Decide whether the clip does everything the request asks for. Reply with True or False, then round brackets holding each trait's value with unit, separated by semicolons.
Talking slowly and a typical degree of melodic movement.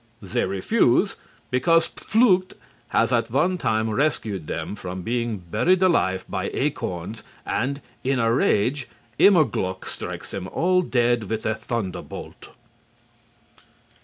False (120 wpm; 7.9 semitones)